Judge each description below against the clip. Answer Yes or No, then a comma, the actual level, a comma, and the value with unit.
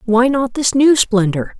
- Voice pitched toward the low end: No, high, 240 Hz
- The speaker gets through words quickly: No, average, 190 wpm